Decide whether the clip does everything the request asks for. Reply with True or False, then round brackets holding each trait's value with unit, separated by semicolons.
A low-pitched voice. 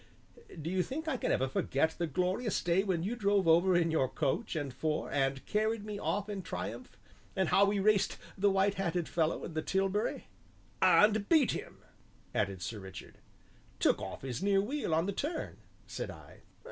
False (185 Hz)